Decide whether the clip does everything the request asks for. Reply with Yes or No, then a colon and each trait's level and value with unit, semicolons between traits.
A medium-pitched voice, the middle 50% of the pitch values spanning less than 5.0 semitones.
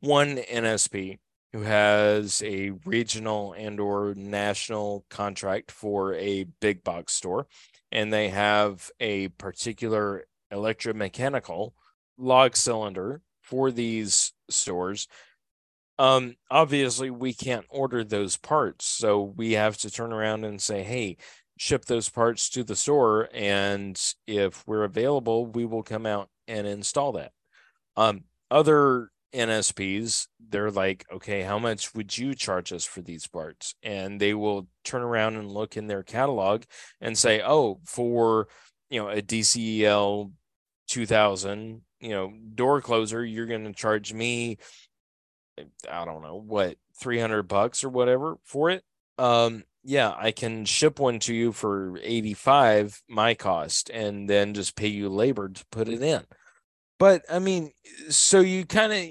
No: low, 110 Hz; average, 2.8 semitones